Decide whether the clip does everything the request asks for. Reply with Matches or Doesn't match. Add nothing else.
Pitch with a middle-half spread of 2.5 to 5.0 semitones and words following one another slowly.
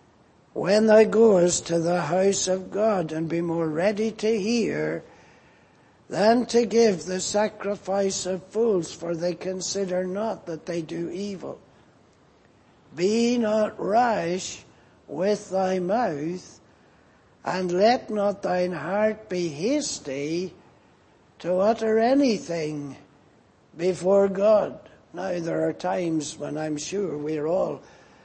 Matches